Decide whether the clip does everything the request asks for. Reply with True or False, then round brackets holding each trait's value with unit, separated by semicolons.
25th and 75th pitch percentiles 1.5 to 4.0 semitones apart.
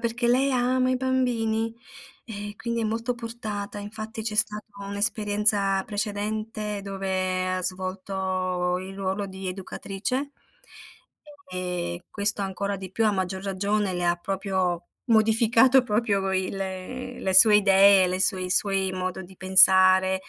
True (2.7 semitones)